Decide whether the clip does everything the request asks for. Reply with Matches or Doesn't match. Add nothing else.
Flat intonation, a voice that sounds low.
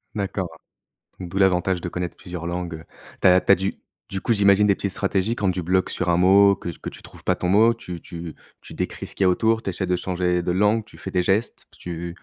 Matches